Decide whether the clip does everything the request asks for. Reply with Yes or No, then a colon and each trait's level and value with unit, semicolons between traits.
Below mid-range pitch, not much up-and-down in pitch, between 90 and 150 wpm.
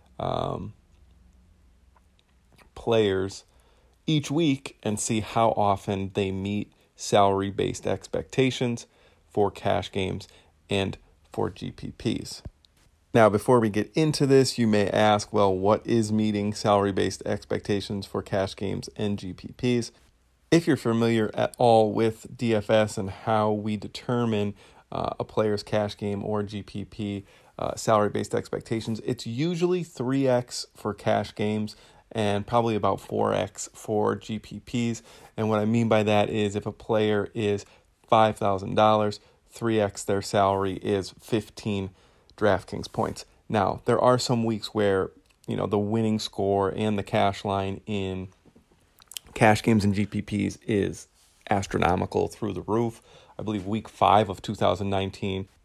Yes: low, 105 Hz; narrow, 2.3 semitones; slow, 135 wpm